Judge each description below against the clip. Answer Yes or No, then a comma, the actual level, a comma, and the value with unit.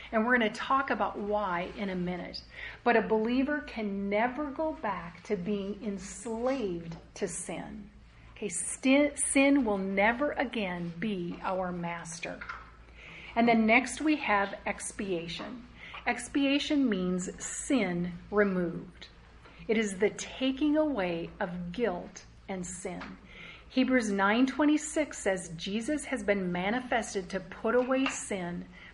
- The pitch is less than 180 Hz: No, high, 210 Hz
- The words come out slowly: Yes, slow, 125 wpm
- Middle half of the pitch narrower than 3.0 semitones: No, average, 5.2 semitones